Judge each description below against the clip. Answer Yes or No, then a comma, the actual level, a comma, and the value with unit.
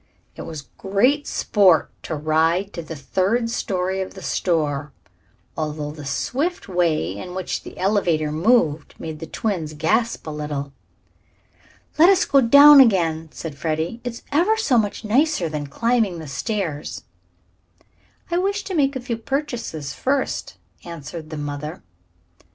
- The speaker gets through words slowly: No, average, 145 wpm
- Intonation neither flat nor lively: No, wide, 7.5 semitones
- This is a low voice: No, medium, 180 Hz